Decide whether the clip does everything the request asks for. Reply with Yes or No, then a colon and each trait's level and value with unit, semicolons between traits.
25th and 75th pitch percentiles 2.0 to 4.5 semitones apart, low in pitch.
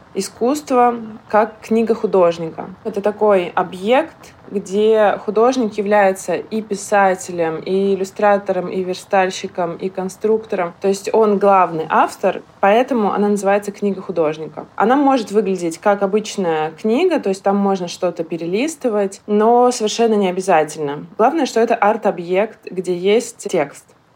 No: average, 2.8 semitones; high, 200 Hz